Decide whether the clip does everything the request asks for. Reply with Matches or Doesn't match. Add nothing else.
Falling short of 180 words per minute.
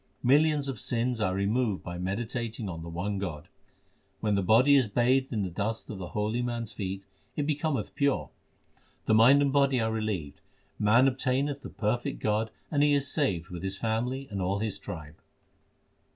Doesn't match